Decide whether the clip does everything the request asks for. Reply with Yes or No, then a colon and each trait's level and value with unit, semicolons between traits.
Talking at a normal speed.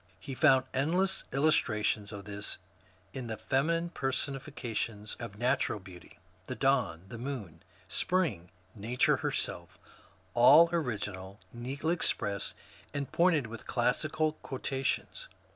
No: slow, 125 wpm